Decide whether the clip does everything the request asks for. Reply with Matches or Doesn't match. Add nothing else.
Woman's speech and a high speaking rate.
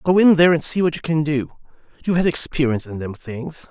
Doesn't match